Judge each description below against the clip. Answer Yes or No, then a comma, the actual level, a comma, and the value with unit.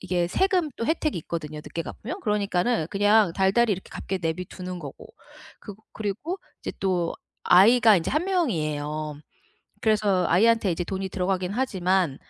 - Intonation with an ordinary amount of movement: Yes, average, 4.3 semitones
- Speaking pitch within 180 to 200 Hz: Yes, high, 190 Hz